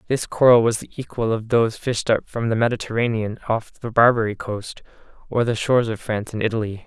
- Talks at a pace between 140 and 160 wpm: No, average, 200 wpm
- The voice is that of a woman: No, male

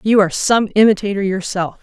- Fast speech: No, average, 165 wpm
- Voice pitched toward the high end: Yes, high, 200 Hz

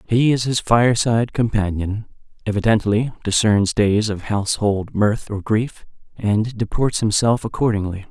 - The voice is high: No, low, 110 Hz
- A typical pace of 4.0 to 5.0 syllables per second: Yes, 4.3 syllables/s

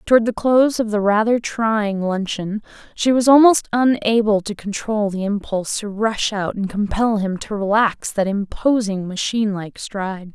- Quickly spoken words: No, average, 170 wpm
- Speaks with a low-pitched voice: No, high, 210 Hz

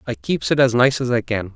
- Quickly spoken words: Yes, fast, 310 wpm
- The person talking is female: No, male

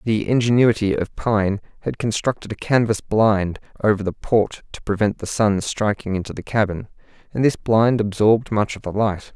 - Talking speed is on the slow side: No, average, 180 wpm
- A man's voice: Yes, male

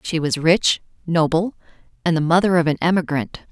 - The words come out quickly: No, average, 170 wpm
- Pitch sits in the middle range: Yes, medium, 165 Hz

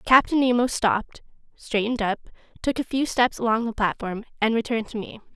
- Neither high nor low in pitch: No, high, 230 Hz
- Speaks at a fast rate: No, average, 180 wpm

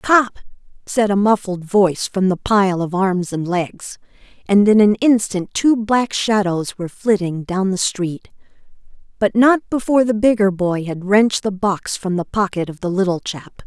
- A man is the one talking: No, female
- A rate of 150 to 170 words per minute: No, average, 180 wpm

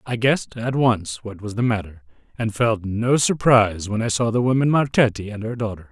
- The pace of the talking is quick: Yes, fast, 215 wpm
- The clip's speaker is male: Yes, male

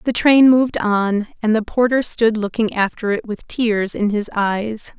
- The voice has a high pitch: Yes, high, 220 Hz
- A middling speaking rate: Yes, average, 195 wpm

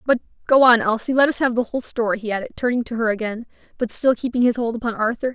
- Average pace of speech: No, fast, 260 wpm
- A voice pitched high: Yes, high, 235 Hz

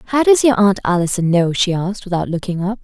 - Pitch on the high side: Yes, high, 195 Hz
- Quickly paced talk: Yes, fast, 235 wpm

